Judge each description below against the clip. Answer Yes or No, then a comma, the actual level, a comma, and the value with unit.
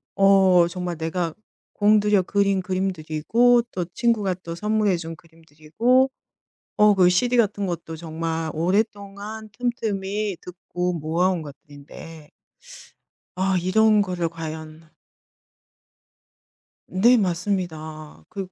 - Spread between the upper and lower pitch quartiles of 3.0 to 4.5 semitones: Yes, average, 4.0 semitones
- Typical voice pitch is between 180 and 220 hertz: Yes, medium, 185 Hz